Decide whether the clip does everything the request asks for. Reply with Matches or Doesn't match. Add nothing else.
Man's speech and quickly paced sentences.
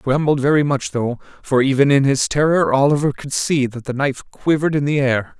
Matches